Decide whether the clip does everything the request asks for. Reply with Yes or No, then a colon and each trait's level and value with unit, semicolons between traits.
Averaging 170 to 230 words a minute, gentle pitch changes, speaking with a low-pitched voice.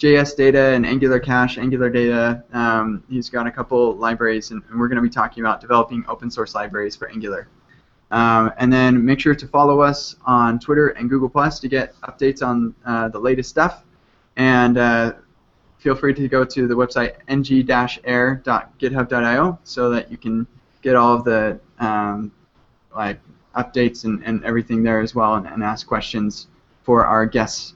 Yes: average, 175 wpm; narrow, 2.3 semitones; low, 120 Hz